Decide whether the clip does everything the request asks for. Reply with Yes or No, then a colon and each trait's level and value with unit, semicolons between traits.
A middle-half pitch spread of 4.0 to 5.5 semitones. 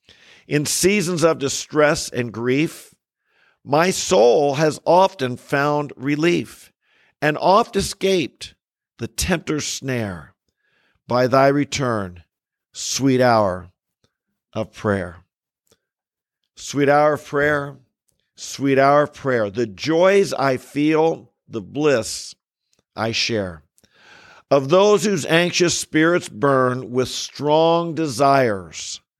Yes: average, 4.5 semitones